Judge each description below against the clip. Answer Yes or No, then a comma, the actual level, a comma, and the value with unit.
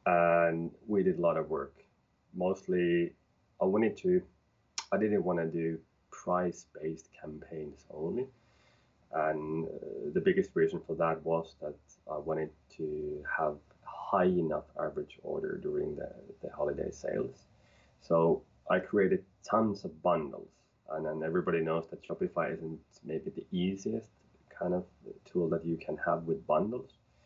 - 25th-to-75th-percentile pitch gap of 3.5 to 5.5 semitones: No, narrow, 2.5 semitones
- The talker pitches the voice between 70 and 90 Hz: Yes, very low, 85 Hz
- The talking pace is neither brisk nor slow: Yes, average, 145 wpm